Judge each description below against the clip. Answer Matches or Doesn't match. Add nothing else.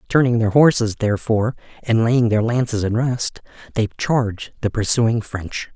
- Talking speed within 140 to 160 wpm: Matches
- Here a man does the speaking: Matches